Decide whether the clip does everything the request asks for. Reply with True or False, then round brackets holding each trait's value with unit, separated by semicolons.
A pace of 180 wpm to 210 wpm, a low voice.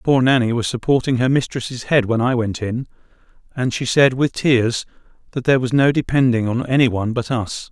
True (200 wpm; 125 Hz)